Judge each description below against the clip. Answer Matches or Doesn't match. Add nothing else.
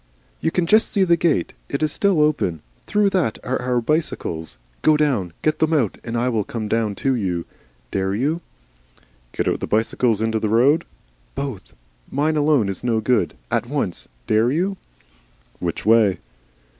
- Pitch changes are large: Matches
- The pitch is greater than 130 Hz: Doesn't match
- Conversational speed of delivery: Matches